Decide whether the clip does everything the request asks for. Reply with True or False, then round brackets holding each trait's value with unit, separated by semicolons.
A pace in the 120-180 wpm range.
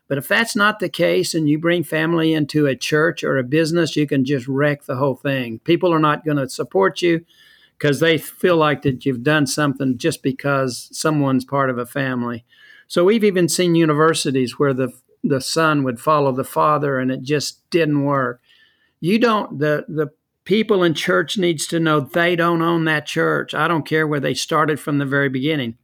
False (205 wpm)